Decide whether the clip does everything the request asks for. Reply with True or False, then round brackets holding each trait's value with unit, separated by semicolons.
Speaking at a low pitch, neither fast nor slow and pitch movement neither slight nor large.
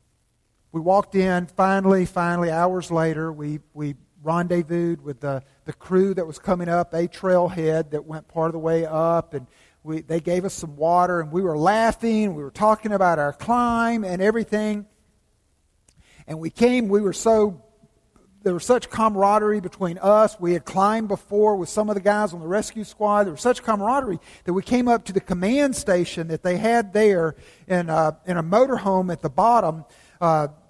False (180 Hz; 190 wpm; 4.4 semitones)